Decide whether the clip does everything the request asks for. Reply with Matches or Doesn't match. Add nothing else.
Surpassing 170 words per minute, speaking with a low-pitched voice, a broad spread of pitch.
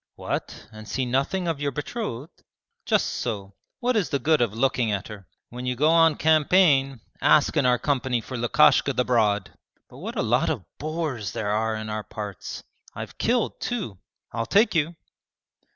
Matches